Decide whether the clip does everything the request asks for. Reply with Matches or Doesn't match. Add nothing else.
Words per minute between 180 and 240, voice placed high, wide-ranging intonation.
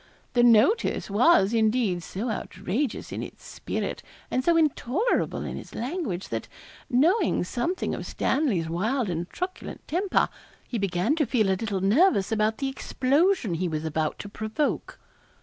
Doesn't match